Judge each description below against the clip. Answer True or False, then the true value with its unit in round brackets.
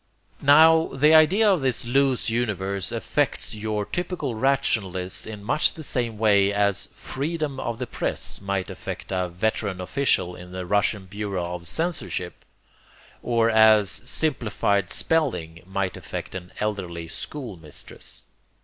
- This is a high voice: False (105 Hz)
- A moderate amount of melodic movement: False (6.3 semitones)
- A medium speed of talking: False (130 wpm)